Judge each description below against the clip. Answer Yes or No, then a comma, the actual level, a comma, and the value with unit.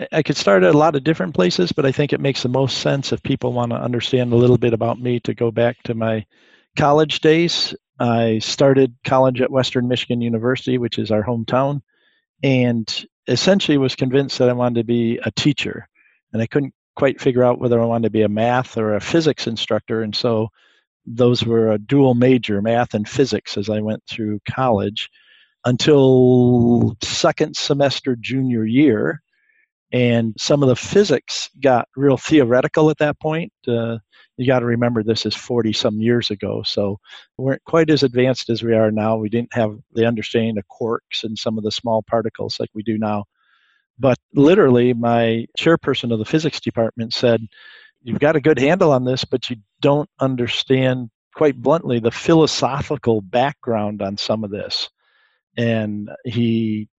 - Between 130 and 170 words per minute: No, average, 180 wpm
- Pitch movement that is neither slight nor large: Yes, average, 3.5 semitones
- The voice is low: Yes, low, 120 Hz